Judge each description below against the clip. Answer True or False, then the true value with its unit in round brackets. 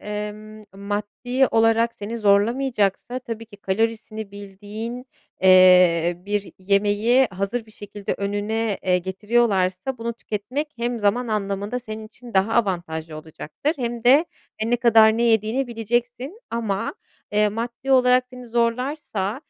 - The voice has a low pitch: False (220 Hz)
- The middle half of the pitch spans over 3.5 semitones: False (3.1 semitones)